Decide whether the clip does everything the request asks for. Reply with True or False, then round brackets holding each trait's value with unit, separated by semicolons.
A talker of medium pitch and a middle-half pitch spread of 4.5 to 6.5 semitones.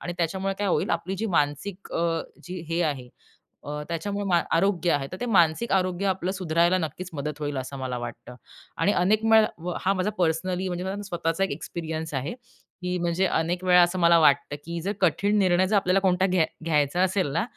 False (175 Hz; 3.0 semitones)